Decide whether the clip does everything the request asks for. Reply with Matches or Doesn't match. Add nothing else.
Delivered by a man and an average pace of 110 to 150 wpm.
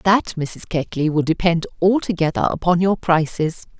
Doesn't match